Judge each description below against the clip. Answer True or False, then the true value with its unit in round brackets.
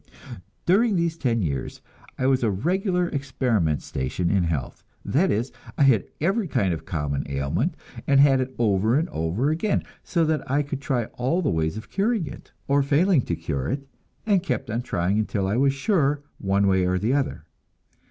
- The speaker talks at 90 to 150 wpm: False (190 wpm)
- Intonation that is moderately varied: False (8.4 semitones)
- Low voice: True (130 Hz)